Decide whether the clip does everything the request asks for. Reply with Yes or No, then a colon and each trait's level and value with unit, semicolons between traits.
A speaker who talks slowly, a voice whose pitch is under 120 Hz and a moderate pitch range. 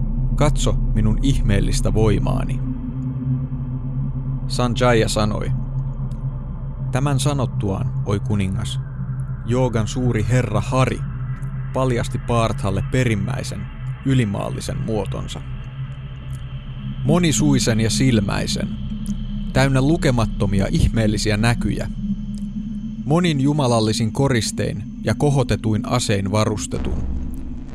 No: slow, 70 wpm; low, 125 Hz; average, 3.1 semitones